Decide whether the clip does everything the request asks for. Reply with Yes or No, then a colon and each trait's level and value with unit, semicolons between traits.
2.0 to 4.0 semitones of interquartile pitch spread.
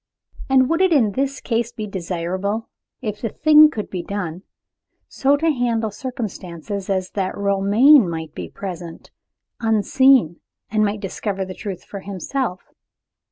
No: average, 5.1 semitones